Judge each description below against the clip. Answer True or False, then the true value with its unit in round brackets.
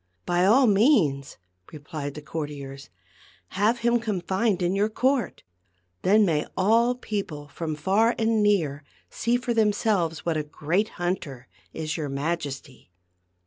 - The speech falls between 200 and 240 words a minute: False (145 wpm)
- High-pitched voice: False (180 Hz)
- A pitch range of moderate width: False (6.5 semitones)